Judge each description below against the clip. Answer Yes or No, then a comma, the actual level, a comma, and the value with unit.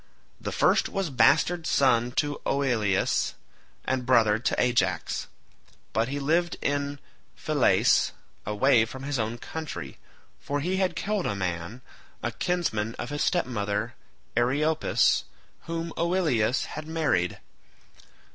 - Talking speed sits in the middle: No, slow, 120 wpm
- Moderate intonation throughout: No, wide, 6.3 semitones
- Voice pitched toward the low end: Yes, low, 130 Hz